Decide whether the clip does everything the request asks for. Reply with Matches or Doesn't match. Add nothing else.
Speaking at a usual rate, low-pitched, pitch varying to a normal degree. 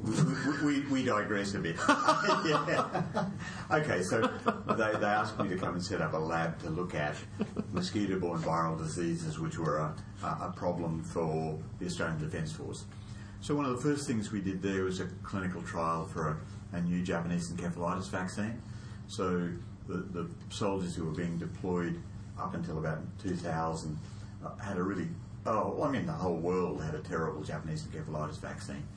Matches